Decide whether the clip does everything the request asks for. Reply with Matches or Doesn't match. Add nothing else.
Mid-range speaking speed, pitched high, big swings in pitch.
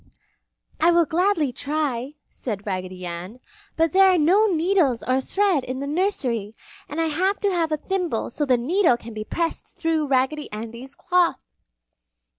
Matches